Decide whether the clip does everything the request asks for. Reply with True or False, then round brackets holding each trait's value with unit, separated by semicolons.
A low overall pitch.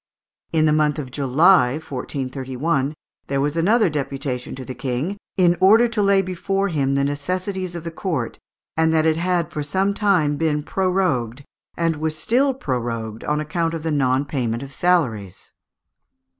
False (155 Hz)